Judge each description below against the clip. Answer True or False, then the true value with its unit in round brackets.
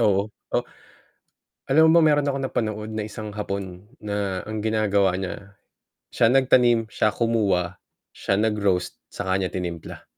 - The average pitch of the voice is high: False (105 Hz)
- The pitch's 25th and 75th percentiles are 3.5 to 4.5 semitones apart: False (2.7 semitones)